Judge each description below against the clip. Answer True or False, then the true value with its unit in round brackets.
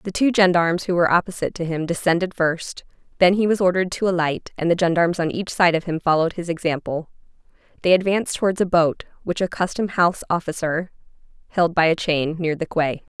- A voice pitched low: False (175 Hz)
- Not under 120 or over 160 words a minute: False (200 wpm)